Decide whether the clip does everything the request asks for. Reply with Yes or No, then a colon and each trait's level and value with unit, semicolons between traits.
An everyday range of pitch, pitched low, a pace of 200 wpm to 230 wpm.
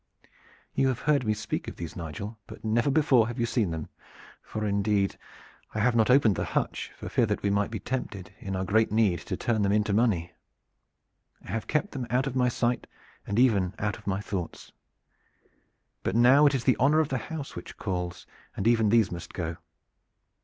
Yes: average, 4.0 semitones; low, 110 Hz; fast, 205 wpm